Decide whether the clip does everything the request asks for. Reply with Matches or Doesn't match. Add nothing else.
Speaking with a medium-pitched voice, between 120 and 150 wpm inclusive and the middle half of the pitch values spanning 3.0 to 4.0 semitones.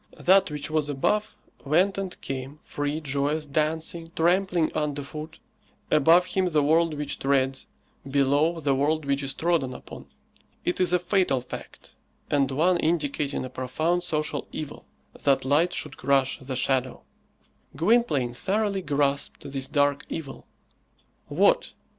Matches